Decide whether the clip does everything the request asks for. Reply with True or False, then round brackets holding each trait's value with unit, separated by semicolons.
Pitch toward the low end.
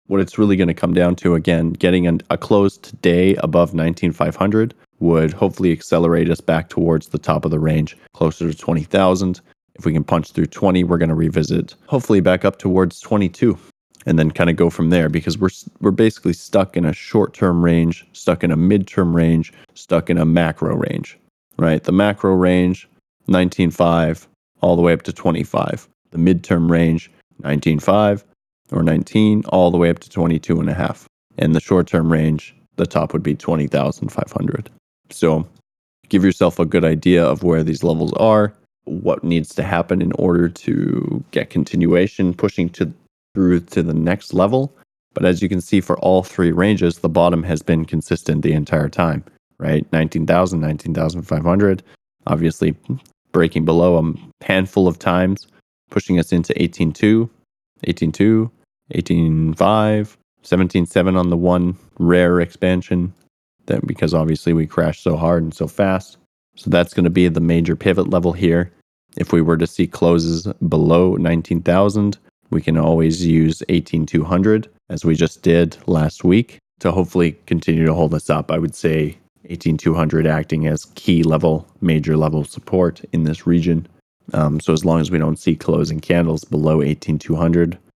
True (85 Hz)